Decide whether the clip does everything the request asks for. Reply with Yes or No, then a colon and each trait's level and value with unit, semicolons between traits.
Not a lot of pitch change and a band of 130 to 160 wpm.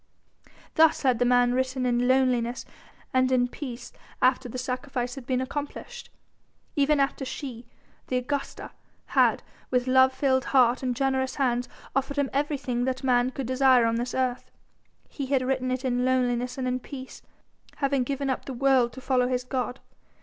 No: narrow, 1.4 semitones; average, 170 wpm